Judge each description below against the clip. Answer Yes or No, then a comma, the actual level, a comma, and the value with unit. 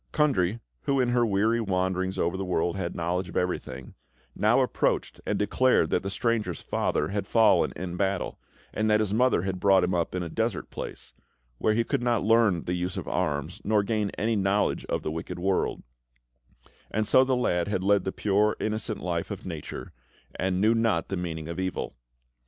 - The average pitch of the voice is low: Yes, very low, 95 Hz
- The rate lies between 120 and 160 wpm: No, average, 195 wpm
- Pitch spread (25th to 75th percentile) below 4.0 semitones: Yes, average, 3.4 semitones